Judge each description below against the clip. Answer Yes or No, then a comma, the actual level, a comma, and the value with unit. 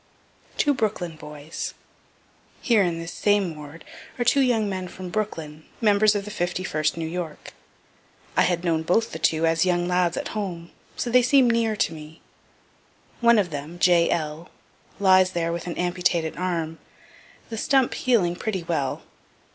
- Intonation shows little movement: No, average, 4.3 semitones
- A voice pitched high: No, medium, 180 Hz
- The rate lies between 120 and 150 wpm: No, average, 165 wpm